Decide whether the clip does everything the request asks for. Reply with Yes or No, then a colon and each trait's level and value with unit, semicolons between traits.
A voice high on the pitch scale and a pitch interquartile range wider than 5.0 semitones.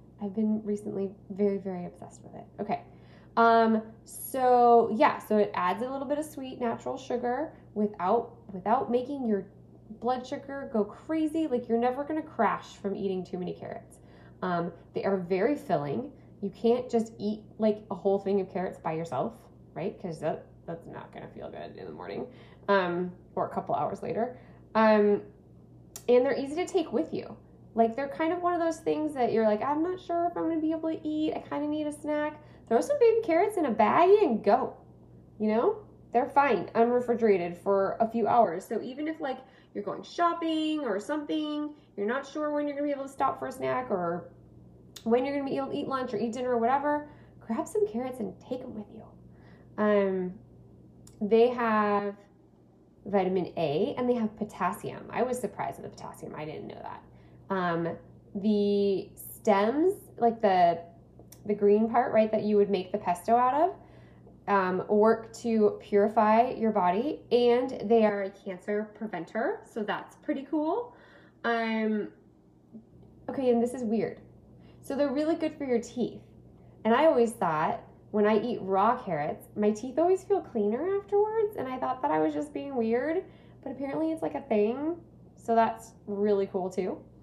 Yes: high, 225 Hz; wide, 5.5 semitones